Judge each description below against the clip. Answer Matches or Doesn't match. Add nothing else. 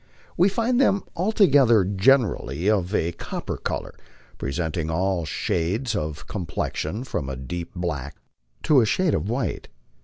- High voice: Doesn't match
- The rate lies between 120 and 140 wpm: Matches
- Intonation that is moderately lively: Doesn't match